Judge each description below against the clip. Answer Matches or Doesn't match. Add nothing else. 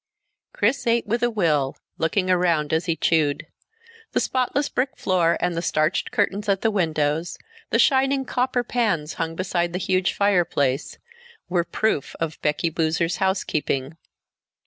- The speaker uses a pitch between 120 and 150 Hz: Doesn't match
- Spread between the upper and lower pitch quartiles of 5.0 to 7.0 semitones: Doesn't match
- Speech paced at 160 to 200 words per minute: Doesn't match